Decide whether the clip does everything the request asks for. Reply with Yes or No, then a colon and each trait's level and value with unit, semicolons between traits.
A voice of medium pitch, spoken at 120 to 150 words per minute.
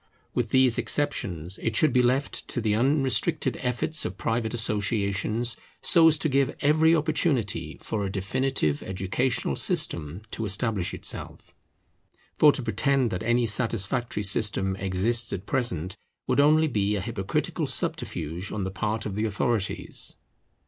No: low, 115 Hz; average, 145 wpm